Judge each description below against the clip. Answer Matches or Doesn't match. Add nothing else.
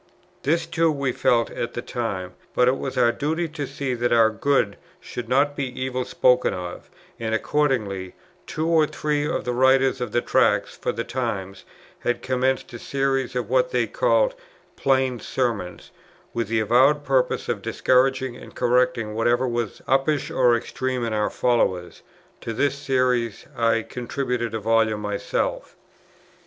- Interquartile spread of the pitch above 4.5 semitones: Doesn't match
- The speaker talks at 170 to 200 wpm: Doesn't match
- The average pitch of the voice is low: Matches